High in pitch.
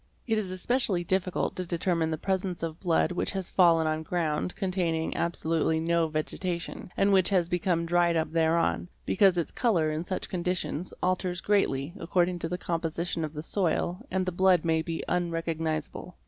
No: medium, 175 Hz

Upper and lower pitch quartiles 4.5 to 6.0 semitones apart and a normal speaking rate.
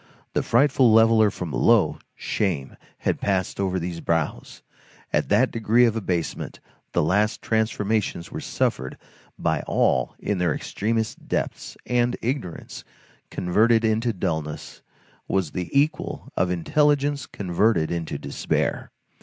No: average, 4.8 semitones; slow, 125 wpm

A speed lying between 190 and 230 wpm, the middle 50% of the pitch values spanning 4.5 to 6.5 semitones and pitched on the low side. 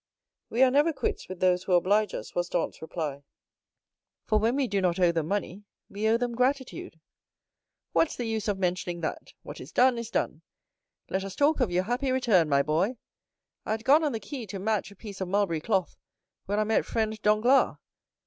No: fast, 205 wpm; average, 4.8 semitones; high, 210 Hz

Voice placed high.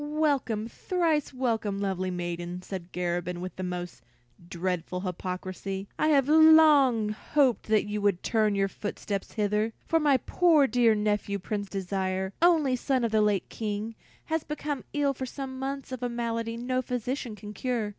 Yes: high, 220 Hz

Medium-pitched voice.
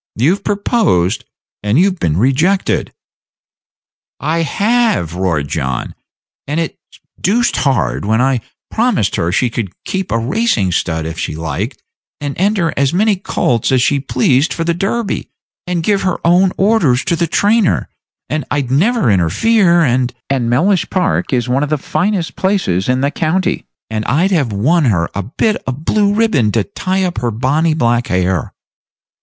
Yes: medium, 145 Hz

